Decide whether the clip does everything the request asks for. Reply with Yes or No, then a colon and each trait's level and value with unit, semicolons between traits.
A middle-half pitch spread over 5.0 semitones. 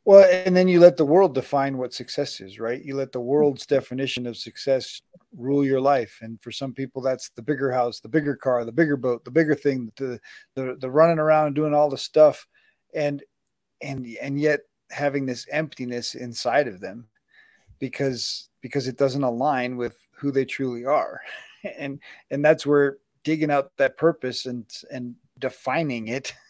No: average, 3.0 semitones